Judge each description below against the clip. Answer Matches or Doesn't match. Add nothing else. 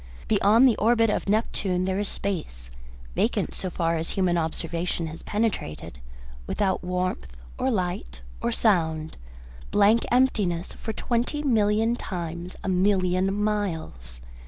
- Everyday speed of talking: Doesn't match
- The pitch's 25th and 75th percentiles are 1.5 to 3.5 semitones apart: Doesn't match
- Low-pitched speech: Doesn't match